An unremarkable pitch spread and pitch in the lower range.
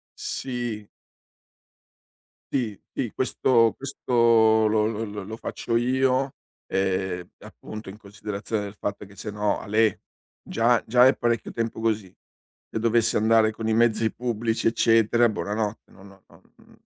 No: narrow, 2.1 semitones; low, 110 Hz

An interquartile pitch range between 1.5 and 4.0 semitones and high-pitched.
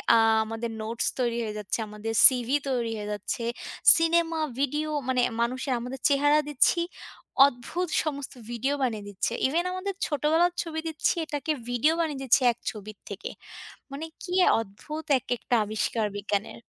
No: wide, 5.4 semitones; very high, 255 Hz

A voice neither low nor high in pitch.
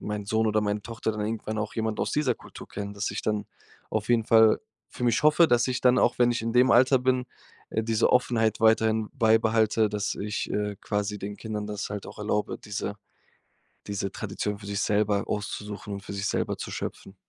No: low, 110 Hz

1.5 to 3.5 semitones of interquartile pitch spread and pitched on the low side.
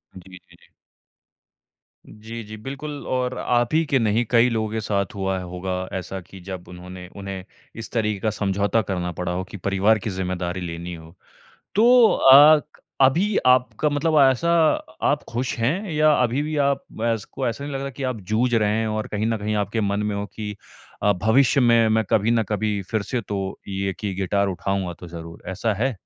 No: average, 4.7 semitones; low, 110 Hz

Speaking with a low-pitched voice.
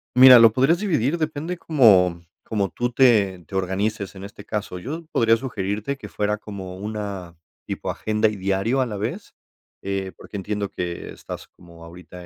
Yes: low, 105 Hz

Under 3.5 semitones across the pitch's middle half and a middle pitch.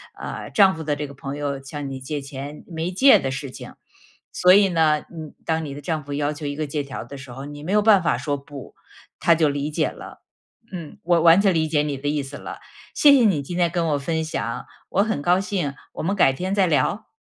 No: average, 3.8 semitones; medium, 150 Hz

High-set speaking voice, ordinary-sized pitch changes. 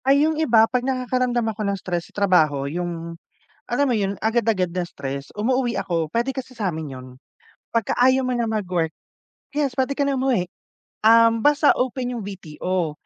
No: high, 220 Hz; wide, 6.3 semitones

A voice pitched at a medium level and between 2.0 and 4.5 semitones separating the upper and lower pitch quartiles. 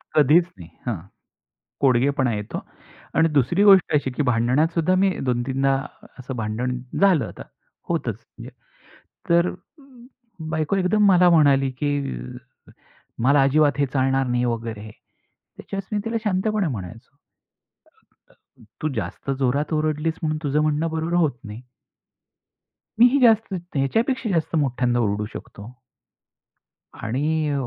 No: medium, 145 Hz; average, 5.2 semitones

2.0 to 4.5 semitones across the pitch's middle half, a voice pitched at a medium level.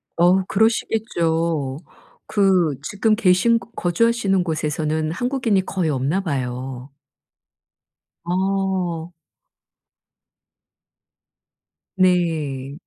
Yes: average, 4.0 semitones; medium, 175 Hz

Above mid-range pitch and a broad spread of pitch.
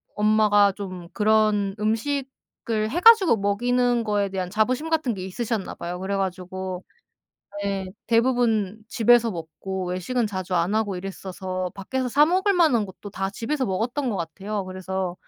No: high, 205 Hz; average, 4.2 semitones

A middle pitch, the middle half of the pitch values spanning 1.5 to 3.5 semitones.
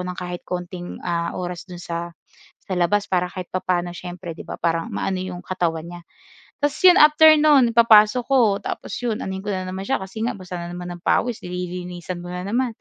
Yes: medium, 180 Hz; average, 3.2 semitones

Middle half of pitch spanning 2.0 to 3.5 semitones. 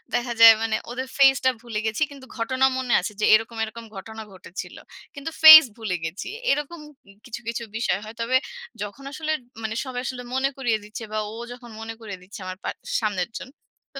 Yes: average, 3.2 semitones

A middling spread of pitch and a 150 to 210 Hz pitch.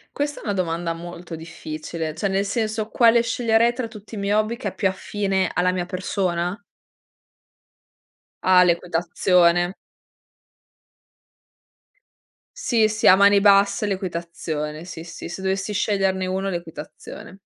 Yes: average, 3.1 semitones; high, 190 Hz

